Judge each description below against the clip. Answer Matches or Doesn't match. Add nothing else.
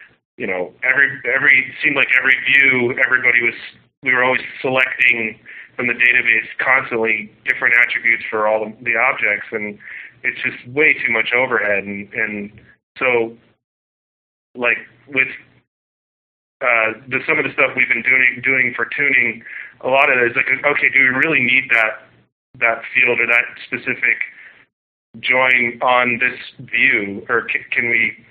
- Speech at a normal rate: Matches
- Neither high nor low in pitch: Doesn't match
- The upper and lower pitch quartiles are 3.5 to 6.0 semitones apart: Doesn't match